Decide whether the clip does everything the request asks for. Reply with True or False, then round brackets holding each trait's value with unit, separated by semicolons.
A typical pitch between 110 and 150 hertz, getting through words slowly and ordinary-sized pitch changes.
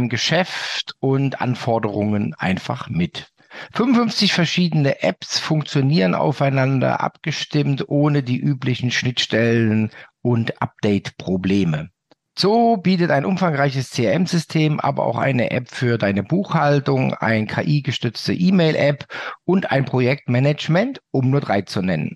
True (140 Hz; 110 wpm; 4.9 semitones)